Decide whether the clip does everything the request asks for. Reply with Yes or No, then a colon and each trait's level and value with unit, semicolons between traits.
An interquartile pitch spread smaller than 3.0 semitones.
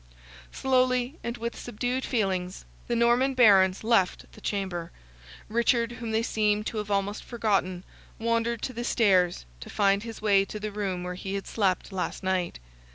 No: average, 3.5 semitones